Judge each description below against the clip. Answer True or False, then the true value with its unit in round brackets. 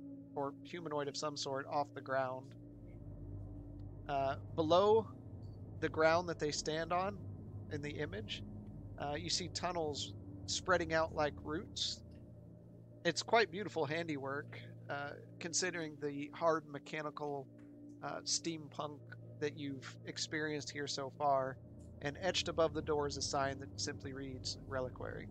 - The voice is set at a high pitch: False (140 Hz)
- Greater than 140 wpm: False (135 wpm)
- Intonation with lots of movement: True (6.3 semitones)